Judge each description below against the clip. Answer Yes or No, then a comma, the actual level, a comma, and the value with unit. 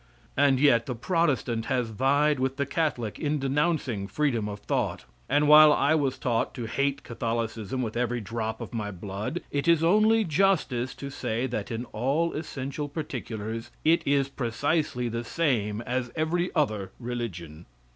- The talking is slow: No, average, 160 wpm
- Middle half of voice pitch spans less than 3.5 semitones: No, average, 4.5 semitones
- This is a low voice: Yes, low, 130 Hz